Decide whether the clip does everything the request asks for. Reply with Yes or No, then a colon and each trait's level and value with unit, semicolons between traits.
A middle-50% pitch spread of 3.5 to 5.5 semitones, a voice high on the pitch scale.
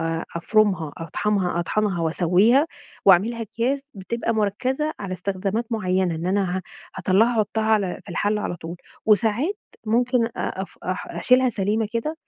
Yes: average, 3.9 semitones; high, 210 Hz